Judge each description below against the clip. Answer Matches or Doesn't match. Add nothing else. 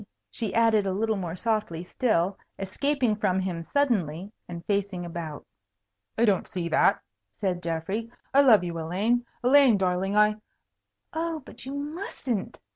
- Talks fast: Doesn't match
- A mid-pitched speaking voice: Doesn't match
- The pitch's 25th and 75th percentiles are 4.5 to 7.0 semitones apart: Matches